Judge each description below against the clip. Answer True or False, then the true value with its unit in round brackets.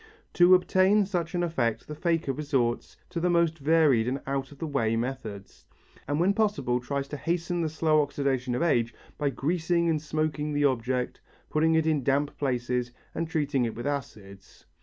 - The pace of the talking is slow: False (180 wpm)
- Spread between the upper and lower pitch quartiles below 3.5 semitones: False (4.5 semitones)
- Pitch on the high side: False (145 Hz)